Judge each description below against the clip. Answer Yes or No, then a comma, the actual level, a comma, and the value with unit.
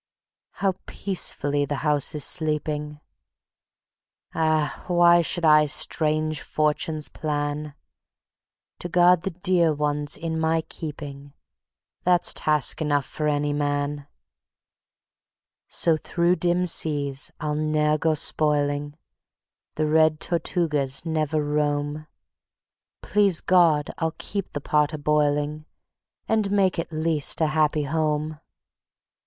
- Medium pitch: Yes, medium, 155 Hz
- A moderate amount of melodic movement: No, narrow, 1.9 semitones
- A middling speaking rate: No, slow, 115 wpm